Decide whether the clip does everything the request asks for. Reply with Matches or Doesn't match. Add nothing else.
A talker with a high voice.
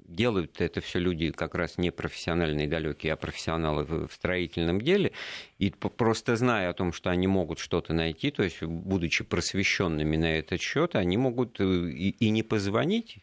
Doesn't match